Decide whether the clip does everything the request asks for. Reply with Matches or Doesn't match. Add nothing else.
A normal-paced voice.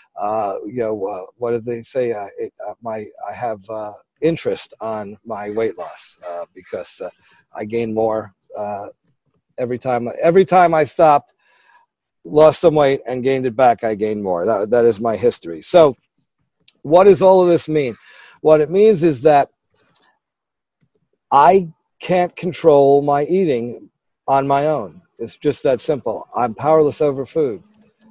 Matches